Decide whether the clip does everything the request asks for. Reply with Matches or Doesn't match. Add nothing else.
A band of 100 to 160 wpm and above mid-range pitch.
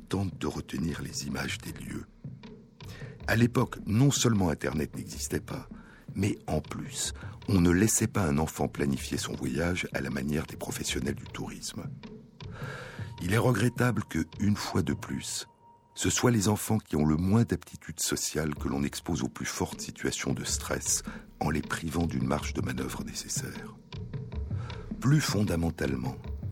Doesn't match